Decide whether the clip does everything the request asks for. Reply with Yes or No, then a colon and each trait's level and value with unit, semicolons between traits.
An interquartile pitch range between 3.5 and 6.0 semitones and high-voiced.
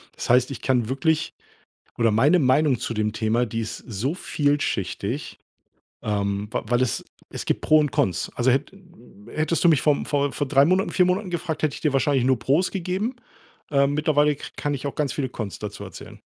No: average, 4.5 semitones; medium, 140 Hz